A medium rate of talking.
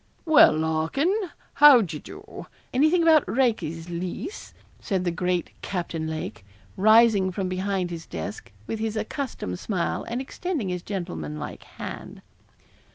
No: slow, 130 wpm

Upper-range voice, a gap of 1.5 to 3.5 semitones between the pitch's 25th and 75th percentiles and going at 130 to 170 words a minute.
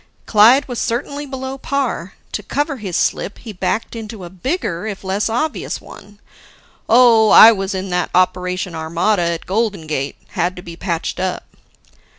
No: high, 205 Hz; average, 4.6 semitones; average, 160 wpm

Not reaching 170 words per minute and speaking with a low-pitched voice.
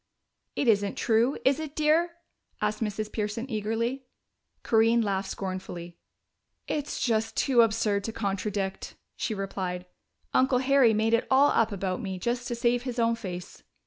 No: average, 150 wpm; high, 225 Hz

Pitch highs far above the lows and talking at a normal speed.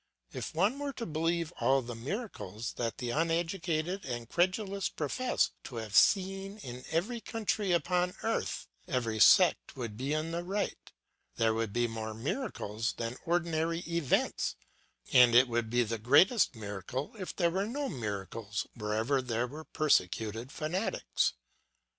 Yes: wide, 7.8 semitones; average, 145 wpm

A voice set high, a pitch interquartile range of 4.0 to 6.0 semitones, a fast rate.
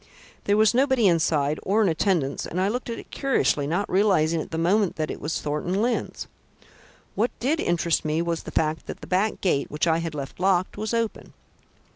No: medium, 180 Hz; average, 5.0 semitones; fast, 210 wpm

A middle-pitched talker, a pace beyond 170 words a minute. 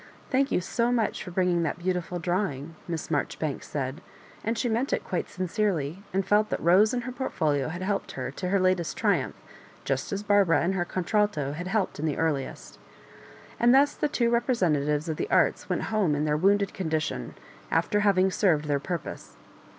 Yes: medium, 180 Hz; average, 195 wpm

